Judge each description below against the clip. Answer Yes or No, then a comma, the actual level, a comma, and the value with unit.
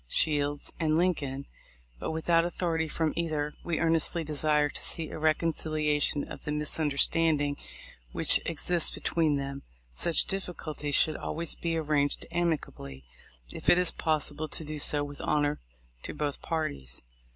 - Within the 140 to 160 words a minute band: Yes, average, 150 wpm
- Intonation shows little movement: Yes, narrow, 2.1 semitones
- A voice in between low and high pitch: Yes, medium, 155 Hz